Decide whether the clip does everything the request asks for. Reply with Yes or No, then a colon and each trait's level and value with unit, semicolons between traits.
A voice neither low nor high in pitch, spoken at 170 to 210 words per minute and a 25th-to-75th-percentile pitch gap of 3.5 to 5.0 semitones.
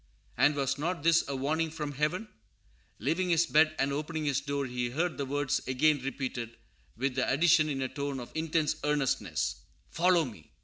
No: medium, 145 Hz; average, 180 wpm; average, 2.9 semitones